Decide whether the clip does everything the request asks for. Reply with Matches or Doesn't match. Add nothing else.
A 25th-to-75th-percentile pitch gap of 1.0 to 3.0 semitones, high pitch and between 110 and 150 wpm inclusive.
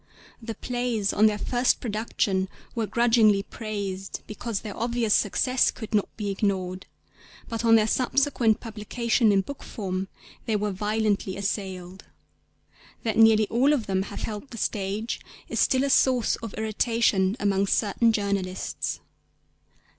Matches